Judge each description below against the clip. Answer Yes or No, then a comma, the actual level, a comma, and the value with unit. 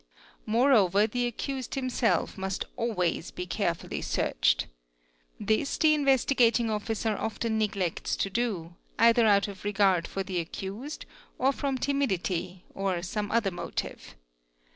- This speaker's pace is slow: Yes, slow, 125 wpm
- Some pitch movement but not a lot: Yes, average, 4.2 semitones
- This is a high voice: Yes, high, 215 Hz